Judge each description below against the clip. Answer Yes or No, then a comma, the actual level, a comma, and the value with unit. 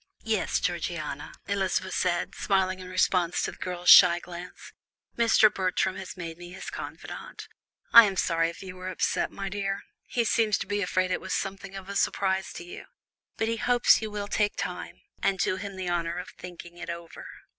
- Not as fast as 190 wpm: No, average, 195 wpm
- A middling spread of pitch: No, narrow, 2.1 semitones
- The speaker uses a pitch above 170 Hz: Yes, medium, 185 Hz